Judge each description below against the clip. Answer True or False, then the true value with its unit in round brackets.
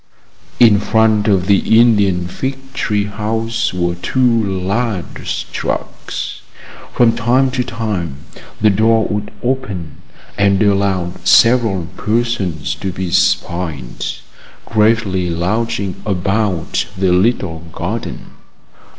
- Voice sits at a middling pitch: False (105 Hz)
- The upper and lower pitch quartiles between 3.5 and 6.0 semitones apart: True (3.9 semitones)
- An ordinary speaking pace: False (105 wpm)